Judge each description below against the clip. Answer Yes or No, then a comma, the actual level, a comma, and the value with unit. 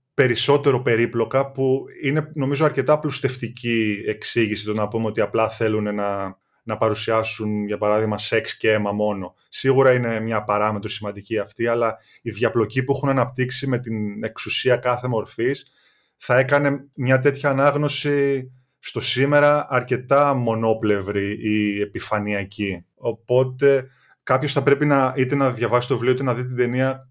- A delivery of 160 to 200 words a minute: No, average, 145 wpm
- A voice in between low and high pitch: No, low, 125 Hz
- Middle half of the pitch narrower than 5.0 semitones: Yes, average, 4.0 semitones